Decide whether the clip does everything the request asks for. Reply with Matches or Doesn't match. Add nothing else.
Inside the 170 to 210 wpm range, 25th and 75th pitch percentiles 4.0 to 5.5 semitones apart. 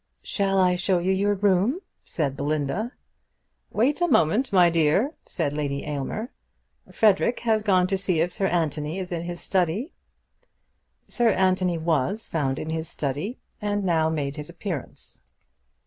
Doesn't match